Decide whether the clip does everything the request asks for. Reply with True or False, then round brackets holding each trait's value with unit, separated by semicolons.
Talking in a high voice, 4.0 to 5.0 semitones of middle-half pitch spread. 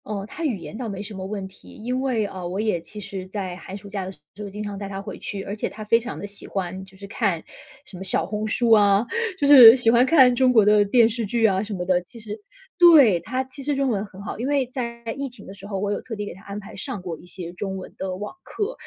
False (210 Hz; 3.6 semitones)